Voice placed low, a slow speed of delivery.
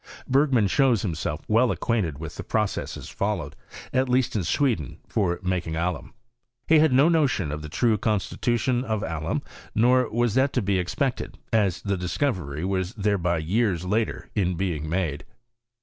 No: low, 100 Hz; average, 160 wpm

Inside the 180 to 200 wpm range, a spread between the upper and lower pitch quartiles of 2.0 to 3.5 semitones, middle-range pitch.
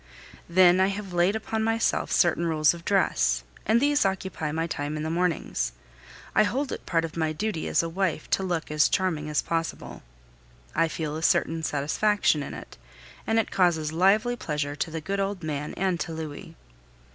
No: average, 190 wpm; average, 3.9 semitones; medium, 170 Hz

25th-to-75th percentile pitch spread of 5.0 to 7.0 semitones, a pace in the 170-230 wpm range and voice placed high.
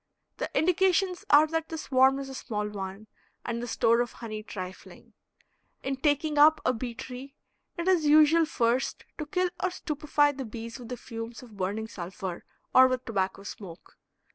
Yes: wide, 5.4 semitones; average, 175 wpm; very high, 255 Hz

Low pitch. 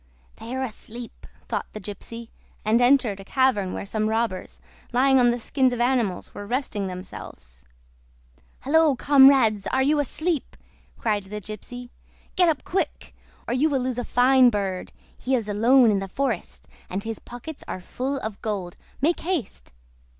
No: high, 240 Hz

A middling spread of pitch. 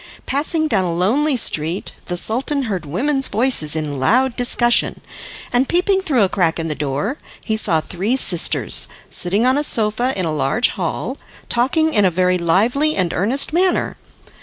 No: wide, 7.4 semitones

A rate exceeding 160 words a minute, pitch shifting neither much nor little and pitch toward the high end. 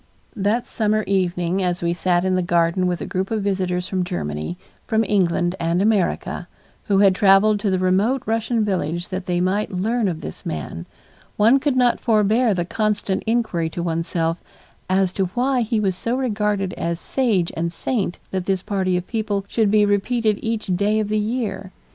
Yes: average, 190 wpm; average, 3.2 semitones; high, 195 Hz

